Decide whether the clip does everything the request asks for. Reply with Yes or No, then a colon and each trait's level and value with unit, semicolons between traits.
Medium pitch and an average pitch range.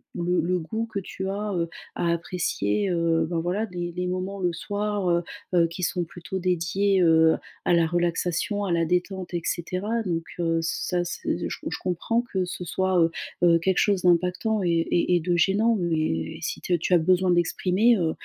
No: medium, 180 Hz; narrow, 2.1 semitones